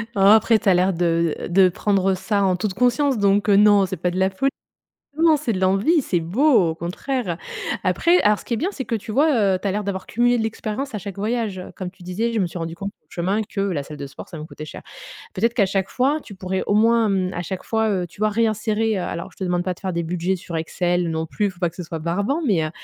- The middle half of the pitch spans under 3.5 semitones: No, average, 3.8 semitones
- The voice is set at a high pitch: Yes, high, 195 Hz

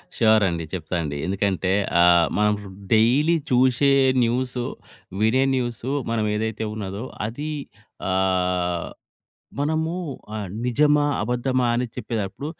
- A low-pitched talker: Yes, low, 110 Hz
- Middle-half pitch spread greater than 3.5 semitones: Yes, average, 5.2 semitones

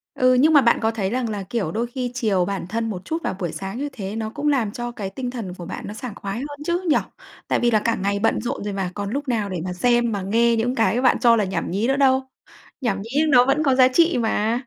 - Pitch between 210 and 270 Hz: Yes, high, 230 Hz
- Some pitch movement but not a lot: Yes, average, 4.1 semitones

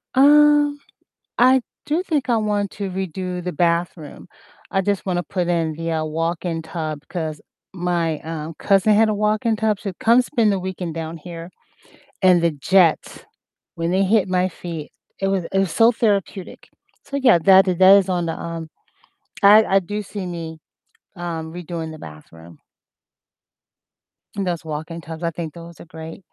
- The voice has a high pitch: No, medium, 180 Hz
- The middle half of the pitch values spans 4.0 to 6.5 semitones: No, average, 3.6 semitones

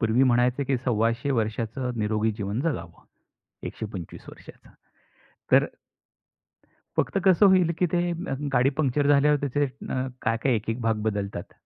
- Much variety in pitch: No, average, 4.3 semitones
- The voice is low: Yes, low, 120 Hz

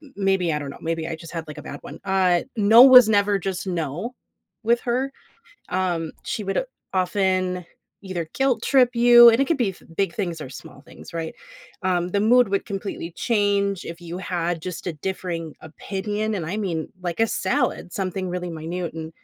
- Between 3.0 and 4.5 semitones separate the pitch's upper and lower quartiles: Yes, average, 3.9 semitones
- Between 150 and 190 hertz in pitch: Yes, medium, 185 Hz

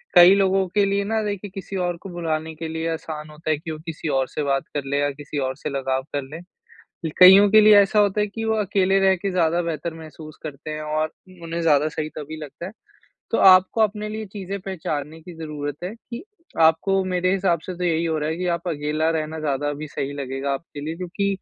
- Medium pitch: Yes, medium, 165 Hz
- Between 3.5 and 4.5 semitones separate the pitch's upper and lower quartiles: Yes, average, 4.0 semitones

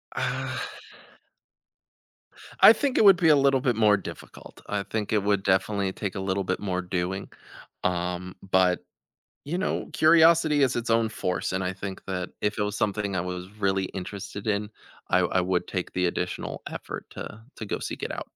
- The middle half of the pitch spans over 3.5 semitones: No, average, 3.1 semitones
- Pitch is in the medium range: No, low, 100 Hz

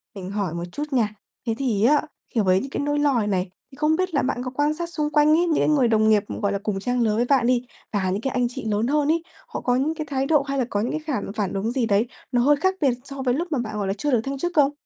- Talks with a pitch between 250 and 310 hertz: Yes, very high, 255 Hz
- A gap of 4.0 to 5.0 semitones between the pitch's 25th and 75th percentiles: No, wide, 5.4 semitones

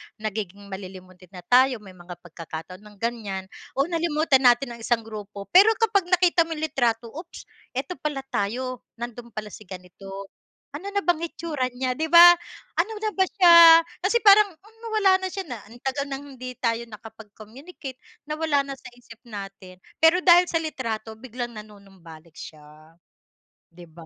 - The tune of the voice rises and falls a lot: Yes, wide, 8.2 semitones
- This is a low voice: No, high, 245 Hz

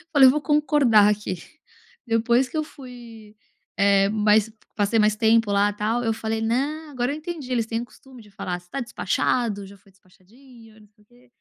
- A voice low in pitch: No, high, 225 Hz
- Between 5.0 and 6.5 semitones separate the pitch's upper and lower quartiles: No, average, 3.4 semitones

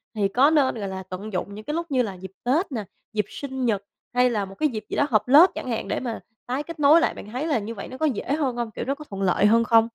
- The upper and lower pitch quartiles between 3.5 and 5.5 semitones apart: Yes, average, 5.2 semitones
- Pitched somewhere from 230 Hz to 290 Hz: Yes, high, 240 Hz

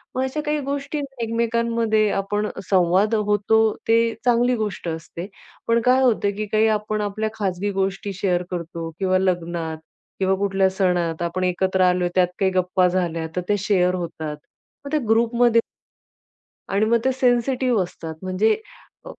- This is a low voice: No, high, 200 Hz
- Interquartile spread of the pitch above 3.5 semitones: Yes, average, 4.1 semitones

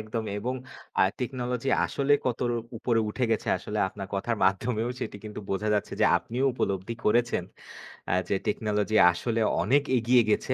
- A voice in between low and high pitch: No, low, 115 Hz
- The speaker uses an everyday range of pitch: Yes, average, 3.0 semitones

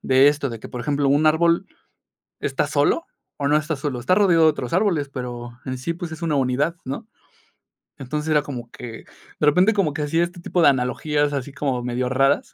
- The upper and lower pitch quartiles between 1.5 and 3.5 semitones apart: No, average, 3.9 semitones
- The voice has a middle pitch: Yes, medium, 145 Hz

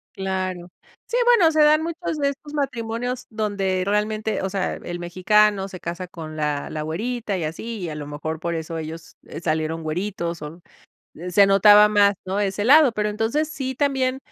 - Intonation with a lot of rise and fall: Yes, wide, 6.2 semitones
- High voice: Yes, high, 200 Hz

